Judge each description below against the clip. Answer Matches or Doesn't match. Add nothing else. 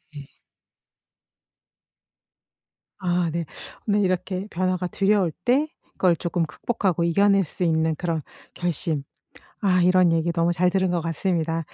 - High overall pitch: Doesn't match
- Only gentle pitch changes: Matches